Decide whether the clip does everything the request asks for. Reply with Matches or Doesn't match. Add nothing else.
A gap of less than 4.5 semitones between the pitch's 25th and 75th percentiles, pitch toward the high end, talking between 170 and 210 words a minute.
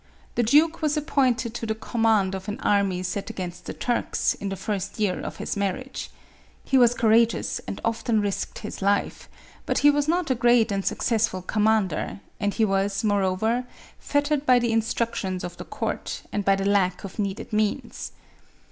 Matches